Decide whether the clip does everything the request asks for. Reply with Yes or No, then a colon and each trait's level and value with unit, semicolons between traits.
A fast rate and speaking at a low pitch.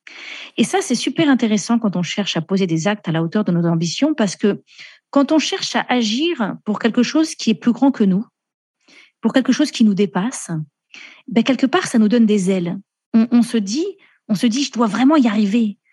No: fast, 225 wpm; high, 230 Hz